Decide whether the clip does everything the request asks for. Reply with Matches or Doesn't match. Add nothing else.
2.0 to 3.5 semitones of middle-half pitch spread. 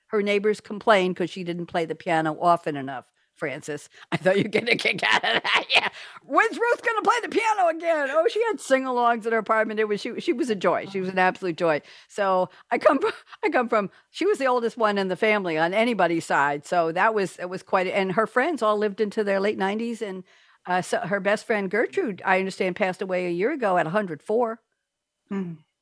Doesn't match